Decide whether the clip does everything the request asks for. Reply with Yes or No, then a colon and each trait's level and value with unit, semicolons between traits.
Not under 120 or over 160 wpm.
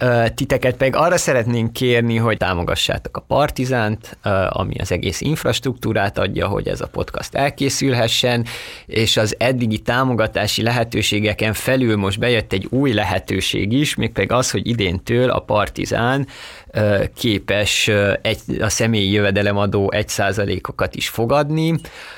Yes: average, 125 wpm